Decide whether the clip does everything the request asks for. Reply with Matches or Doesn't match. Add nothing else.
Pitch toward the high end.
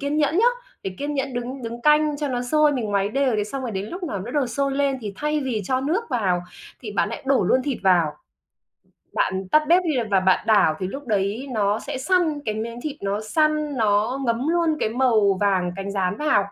Matches